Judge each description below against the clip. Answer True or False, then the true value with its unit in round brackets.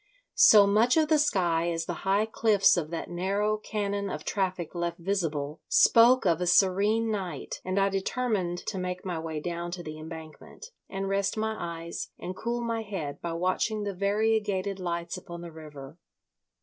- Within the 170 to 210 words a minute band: True (175 wpm)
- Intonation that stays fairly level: False (3.6 semitones)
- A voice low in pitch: False (190 Hz)